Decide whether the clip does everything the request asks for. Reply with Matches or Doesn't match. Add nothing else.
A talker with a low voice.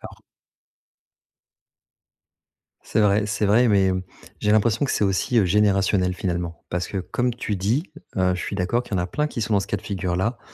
Matches